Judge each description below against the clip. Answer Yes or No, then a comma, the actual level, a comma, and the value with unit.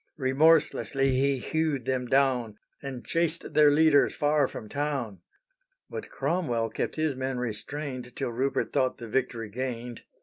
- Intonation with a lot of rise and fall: No, average, 3.1 semitones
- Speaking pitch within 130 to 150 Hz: Yes, low, 135 Hz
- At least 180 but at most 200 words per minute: No, average, 140 wpm